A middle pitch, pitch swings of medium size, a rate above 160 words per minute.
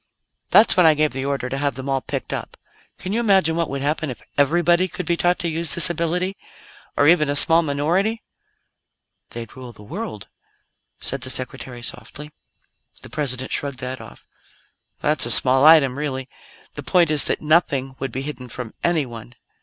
Yes: medium, 145 Hz; average, 4.4 semitones; average, 185 wpm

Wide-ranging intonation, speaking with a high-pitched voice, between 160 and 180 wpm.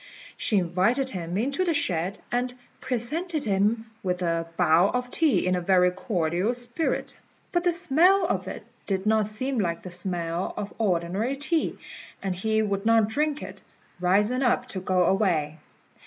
Yes: wide, 5.7 semitones; high, 210 Hz; average, 165 wpm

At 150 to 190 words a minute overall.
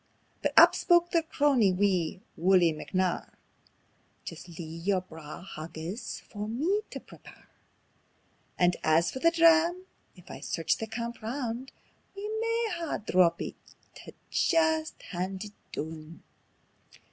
No: slow, 135 wpm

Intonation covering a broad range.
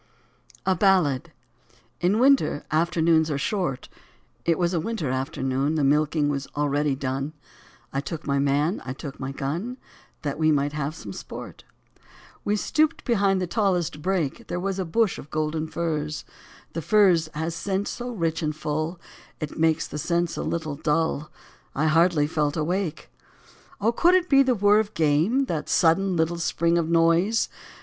No: average, 4.2 semitones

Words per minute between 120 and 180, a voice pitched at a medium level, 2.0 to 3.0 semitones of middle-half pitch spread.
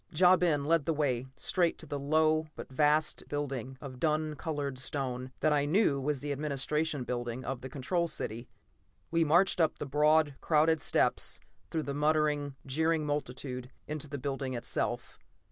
Yes: average, 165 wpm; medium, 145 Hz; average, 2.7 semitones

